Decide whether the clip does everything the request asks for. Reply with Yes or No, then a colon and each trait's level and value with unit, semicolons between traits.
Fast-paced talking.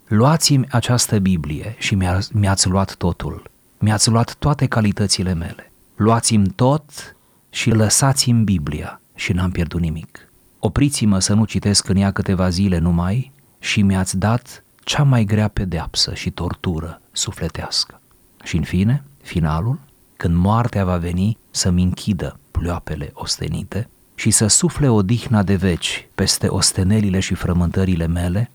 No: average, 135 wpm